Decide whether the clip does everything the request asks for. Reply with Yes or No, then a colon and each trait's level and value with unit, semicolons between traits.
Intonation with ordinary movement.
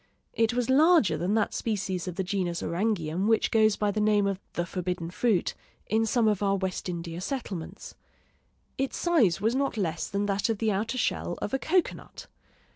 Yes: average, 3.8 semitones